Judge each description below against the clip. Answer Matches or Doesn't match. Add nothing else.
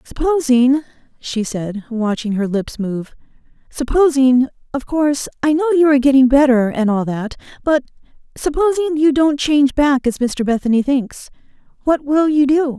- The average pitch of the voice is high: Matches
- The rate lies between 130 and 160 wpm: Matches